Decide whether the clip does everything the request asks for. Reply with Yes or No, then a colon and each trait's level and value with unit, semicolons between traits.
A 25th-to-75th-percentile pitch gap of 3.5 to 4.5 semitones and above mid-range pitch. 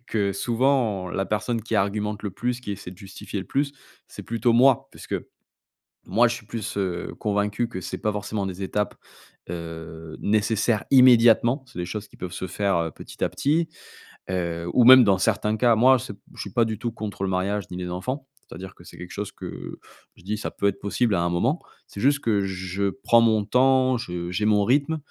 No: average, 3.9 semitones; low, 105 Hz